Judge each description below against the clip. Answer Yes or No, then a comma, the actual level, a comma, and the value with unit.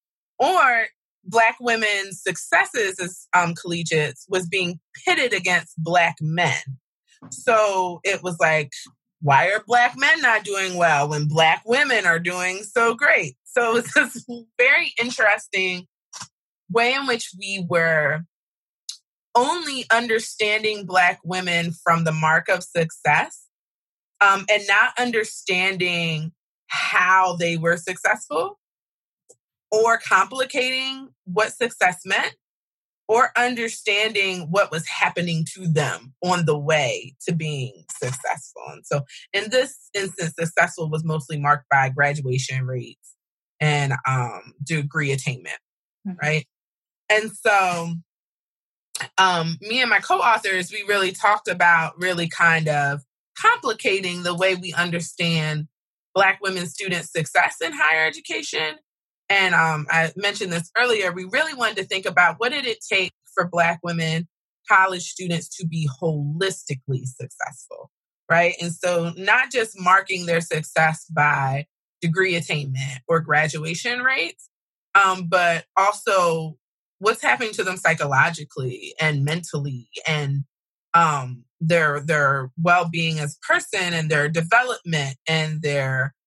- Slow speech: Yes, slow, 125 wpm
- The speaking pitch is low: No, medium, 175 Hz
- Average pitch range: Yes, average, 4.2 semitones